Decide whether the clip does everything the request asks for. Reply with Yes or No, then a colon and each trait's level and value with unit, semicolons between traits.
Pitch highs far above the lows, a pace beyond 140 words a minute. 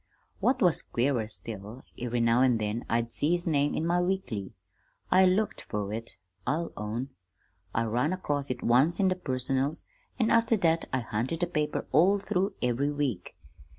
Yes: wide, 7.1 semitones; average, 175 wpm